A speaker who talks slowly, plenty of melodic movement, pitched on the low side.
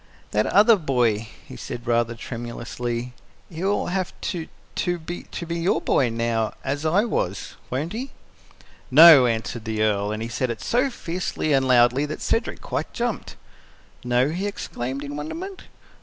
No: average, 155 wpm; wide, 6.5 semitones; low, 130 Hz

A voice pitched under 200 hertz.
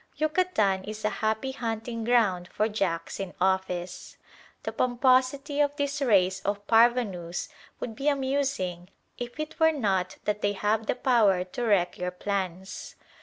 No: high, 215 Hz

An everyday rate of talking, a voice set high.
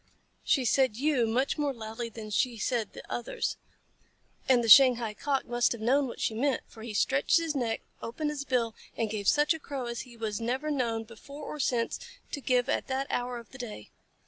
No: fast, 210 wpm; high, 245 Hz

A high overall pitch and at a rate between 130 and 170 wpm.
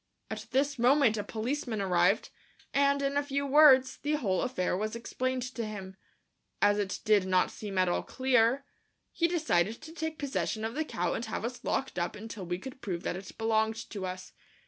No: high, 230 Hz; average, 195 wpm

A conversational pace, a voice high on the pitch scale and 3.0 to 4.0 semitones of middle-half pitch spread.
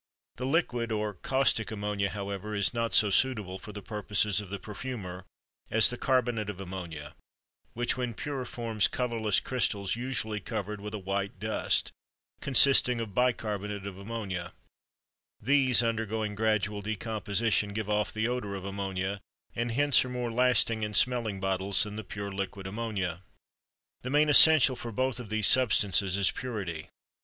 No: average, 155 wpm; low, 105 Hz; average, 3.3 semitones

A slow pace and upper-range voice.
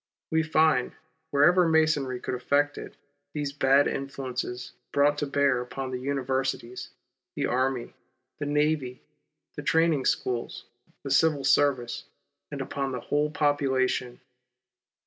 No: slow, 125 wpm; medium, 140 Hz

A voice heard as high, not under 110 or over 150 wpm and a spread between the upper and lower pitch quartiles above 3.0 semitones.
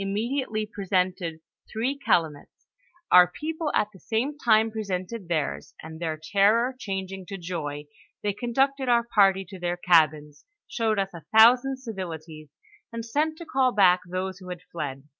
No: high, 195 Hz; average, 160 wpm; average, 5.0 semitones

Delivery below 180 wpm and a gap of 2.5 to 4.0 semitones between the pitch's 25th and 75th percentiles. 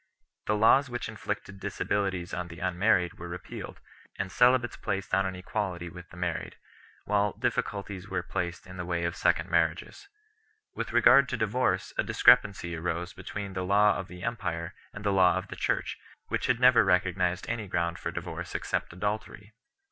No: average, 185 wpm; average, 2.9 semitones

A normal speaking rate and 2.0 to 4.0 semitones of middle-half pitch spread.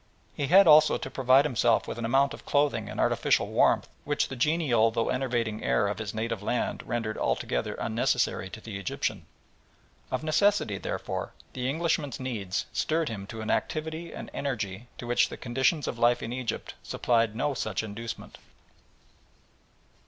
No: average, 160 wpm; average, 4.6 semitones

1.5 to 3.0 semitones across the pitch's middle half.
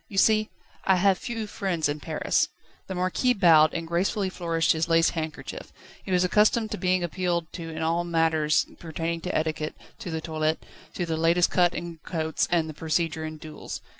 Yes: narrow, 2.4 semitones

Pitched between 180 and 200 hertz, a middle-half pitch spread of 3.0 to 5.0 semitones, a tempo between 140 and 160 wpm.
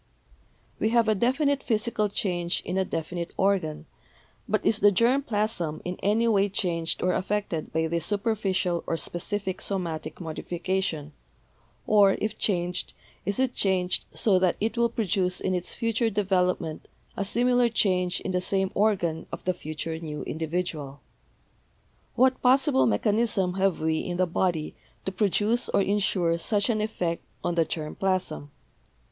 Yes: high, 190 Hz; average, 3.7 semitones; average, 155 wpm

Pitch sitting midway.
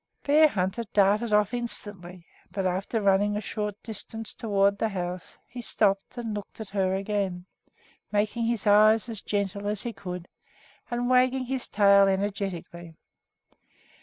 No: high, 205 Hz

